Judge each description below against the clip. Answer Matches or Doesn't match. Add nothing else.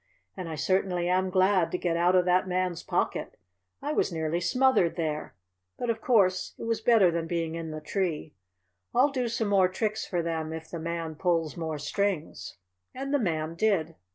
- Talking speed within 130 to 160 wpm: Doesn't match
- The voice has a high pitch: Doesn't match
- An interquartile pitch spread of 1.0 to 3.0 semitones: Doesn't match